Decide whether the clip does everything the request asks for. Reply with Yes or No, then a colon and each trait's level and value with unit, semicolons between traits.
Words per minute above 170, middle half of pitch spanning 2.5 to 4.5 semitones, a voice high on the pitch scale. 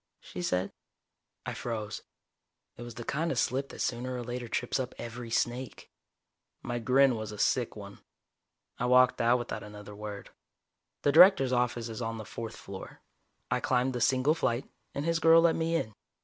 No: average, 180 wpm; average, 2.8 semitones; low, 120 Hz